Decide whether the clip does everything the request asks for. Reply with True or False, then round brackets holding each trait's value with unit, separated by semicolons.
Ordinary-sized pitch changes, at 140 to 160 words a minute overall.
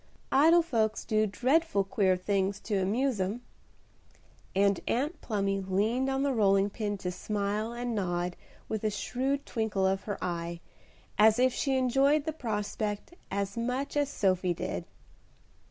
True (4.7 semitones; 150 wpm)